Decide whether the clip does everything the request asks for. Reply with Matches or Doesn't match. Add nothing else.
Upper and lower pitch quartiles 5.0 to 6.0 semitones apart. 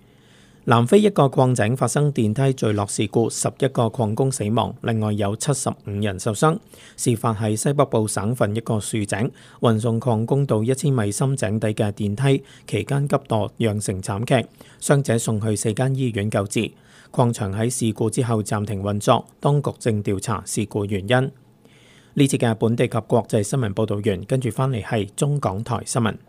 Doesn't match